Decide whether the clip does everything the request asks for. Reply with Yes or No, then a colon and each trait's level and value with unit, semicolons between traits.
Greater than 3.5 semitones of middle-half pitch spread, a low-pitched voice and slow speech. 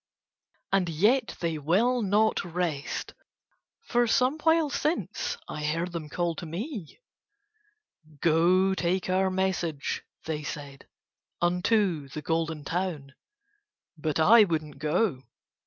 No: average, 4.8 semitones; medium, 175 Hz; slow, 120 wpm